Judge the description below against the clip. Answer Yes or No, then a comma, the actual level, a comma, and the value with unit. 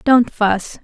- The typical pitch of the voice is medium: No, high, 220 Hz